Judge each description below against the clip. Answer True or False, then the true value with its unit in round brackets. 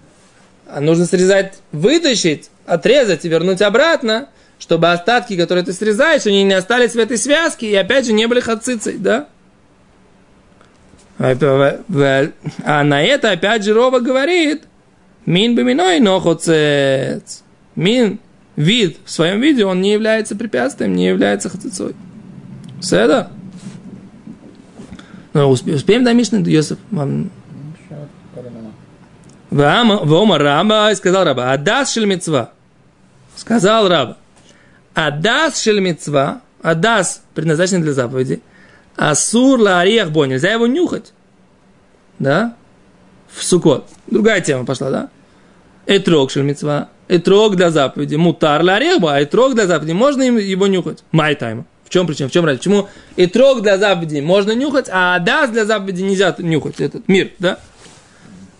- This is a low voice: False (190 Hz)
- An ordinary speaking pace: True (125 wpm)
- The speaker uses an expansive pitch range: True (6.1 semitones)